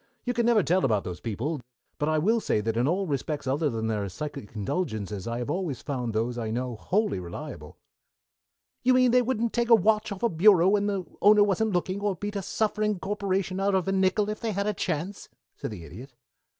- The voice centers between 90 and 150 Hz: No, medium, 185 Hz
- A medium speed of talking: No, fast, 220 wpm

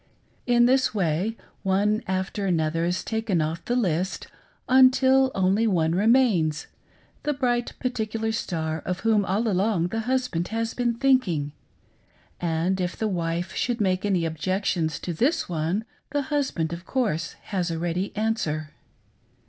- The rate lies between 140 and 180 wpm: Yes, average, 150 wpm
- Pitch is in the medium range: No, high, 195 Hz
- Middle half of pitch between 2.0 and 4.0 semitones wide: No, wide, 5.4 semitones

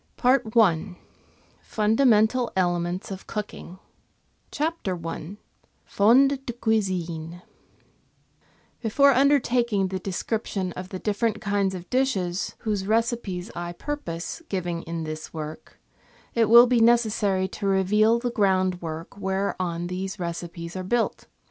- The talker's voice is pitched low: No, high, 195 Hz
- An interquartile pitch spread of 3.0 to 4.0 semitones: No, average, 4.5 semitones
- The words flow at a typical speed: No, slow, 115 wpm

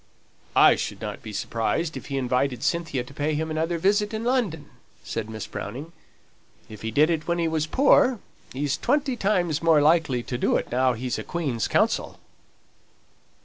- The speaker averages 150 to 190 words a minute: Yes, average, 180 wpm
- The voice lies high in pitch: No, medium, 155 Hz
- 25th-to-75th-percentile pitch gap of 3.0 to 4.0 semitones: No, average, 5.2 semitones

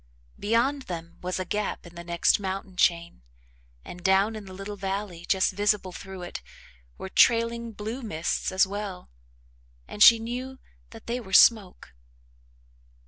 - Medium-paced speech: Yes, average, 150 wpm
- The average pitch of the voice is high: Yes, high, 195 Hz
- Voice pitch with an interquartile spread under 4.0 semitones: Yes, average, 3.5 semitones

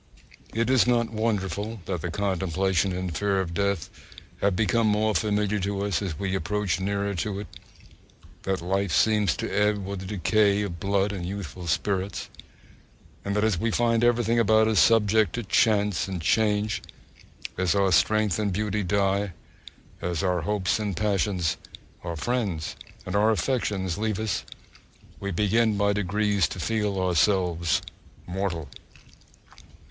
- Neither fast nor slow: Yes, average, 150 wpm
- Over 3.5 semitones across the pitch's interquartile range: No, narrow, 2.4 semitones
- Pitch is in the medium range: No, low, 100 Hz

